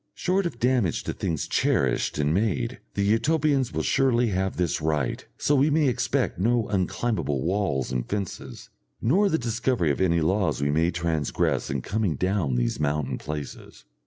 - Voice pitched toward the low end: Yes, very low, 95 Hz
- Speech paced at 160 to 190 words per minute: Yes, average, 165 wpm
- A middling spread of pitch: No, wide, 7.9 semitones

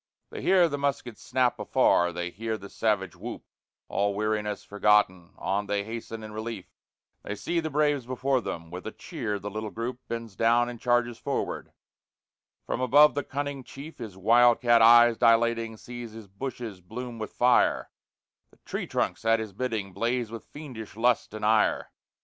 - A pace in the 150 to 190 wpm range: Yes, average, 175 wpm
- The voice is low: Yes, low, 115 Hz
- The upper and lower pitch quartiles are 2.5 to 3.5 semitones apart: Yes, average, 2.9 semitones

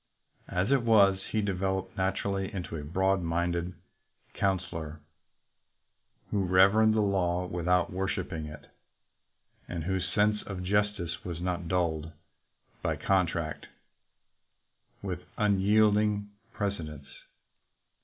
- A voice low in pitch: Yes, very low, 95 Hz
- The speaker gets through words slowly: Yes, slow, 105 wpm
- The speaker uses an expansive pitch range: No, average, 2.7 semitones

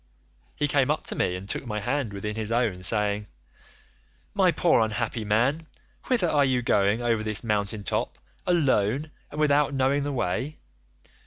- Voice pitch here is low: Yes, low, 120 Hz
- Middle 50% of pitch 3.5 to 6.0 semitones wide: Yes, average, 5.3 semitones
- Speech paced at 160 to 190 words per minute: Yes, average, 165 wpm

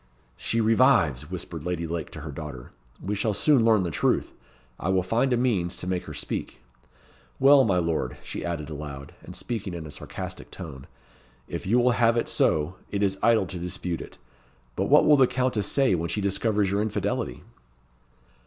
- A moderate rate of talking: Yes, average, 190 wpm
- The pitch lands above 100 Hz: No, very low, 95 Hz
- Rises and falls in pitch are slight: No, wide, 5.6 semitones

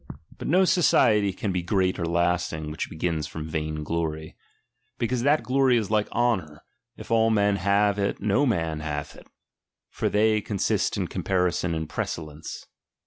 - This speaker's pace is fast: No, average, 165 wpm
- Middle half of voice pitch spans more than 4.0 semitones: Yes, wide, 5.4 semitones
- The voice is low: Yes, very low, 95 Hz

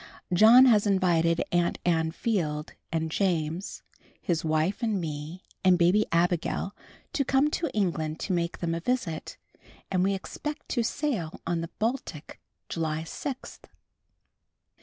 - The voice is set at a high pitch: No, medium, 175 Hz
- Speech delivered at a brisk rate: No, average, 140 wpm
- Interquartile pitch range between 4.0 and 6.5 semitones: Yes, average, 4.7 semitones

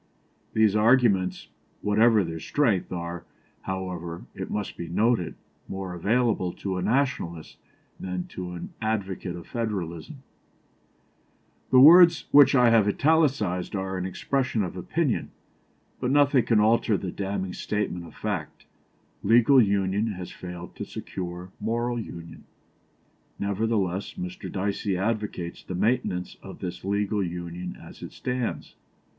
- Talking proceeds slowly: Yes, slow, 130 wpm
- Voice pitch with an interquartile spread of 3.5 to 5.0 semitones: Yes, average, 4.4 semitones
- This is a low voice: Yes, low, 100 Hz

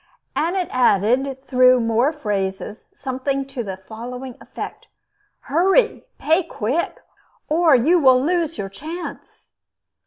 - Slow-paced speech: Yes, slow, 125 wpm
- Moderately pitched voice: No, very high, 265 Hz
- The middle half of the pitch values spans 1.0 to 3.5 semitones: No, wide, 5.4 semitones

